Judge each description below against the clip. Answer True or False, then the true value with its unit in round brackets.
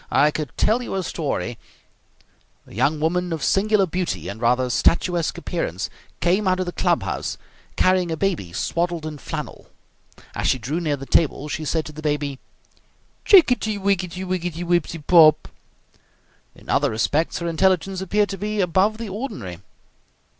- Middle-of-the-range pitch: True (170 Hz)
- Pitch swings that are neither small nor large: True (4.0 semitones)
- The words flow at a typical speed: True (165 wpm)